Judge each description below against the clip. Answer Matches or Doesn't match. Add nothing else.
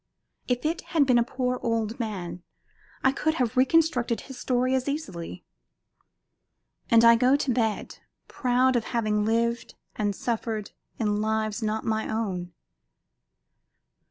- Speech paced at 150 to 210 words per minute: Doesn't match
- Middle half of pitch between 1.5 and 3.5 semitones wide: Matches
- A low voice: Doesn't match